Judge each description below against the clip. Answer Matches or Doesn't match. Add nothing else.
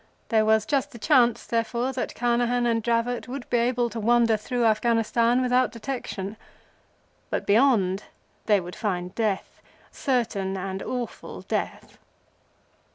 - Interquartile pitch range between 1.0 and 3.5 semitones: Matches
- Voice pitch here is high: Matches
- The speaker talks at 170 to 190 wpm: Doesn't match